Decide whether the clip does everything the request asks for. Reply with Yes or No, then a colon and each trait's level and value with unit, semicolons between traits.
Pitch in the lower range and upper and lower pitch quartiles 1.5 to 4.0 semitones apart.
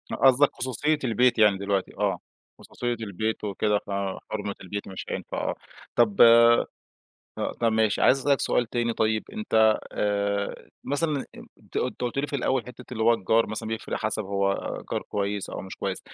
Yes: low, 110 Hz; average, 3.4 semitones